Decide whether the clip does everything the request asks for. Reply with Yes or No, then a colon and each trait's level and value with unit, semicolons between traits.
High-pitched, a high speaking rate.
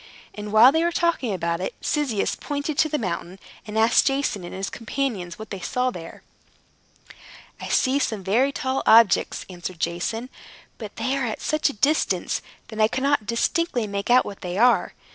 No: high, 230 Hz; average, 180 wpm